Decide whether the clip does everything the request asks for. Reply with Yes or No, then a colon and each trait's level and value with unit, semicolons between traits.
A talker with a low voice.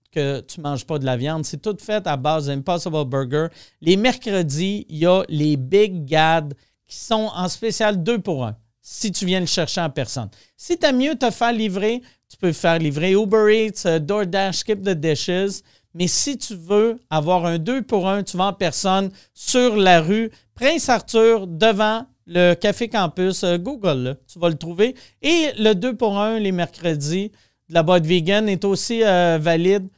No: medium, 185 Hz